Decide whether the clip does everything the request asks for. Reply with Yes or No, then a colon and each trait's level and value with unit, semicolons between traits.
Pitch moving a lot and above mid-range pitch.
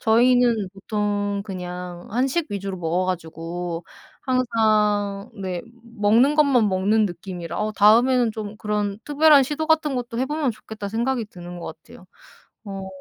No: average, 4.6 semitones; high, 210 Hz